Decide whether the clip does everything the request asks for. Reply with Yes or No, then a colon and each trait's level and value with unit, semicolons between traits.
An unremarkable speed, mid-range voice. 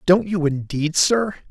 Yes: average, 160 wpm; medium, 175 Hz